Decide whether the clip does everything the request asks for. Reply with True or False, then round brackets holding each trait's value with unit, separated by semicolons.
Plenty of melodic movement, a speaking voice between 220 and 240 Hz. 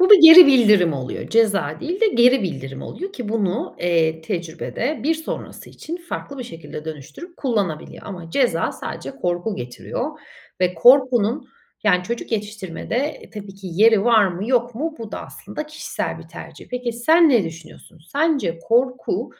True (7.5 semitones; 225 Hz)